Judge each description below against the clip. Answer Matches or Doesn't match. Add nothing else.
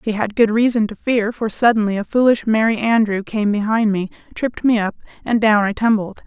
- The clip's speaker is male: Doesn't match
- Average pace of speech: Doesn't match